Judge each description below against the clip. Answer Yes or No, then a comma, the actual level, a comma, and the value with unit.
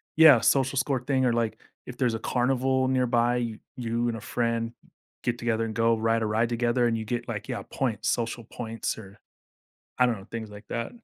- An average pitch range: No, narrow, 1.8 semitones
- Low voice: Yes, low, 120 Hz